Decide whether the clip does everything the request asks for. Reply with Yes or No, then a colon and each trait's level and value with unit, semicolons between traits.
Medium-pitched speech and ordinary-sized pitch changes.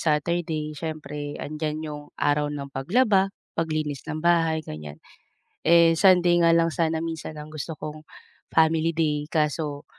No: medium, 155 Hz; narrow, 1.9 semitones